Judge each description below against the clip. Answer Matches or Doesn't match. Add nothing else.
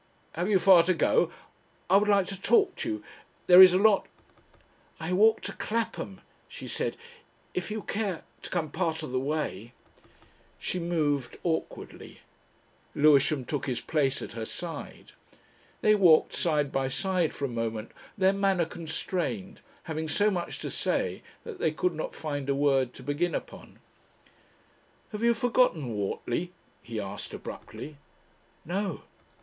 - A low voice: Doesn't match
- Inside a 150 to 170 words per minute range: Matches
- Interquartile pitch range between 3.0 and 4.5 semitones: Doesn't match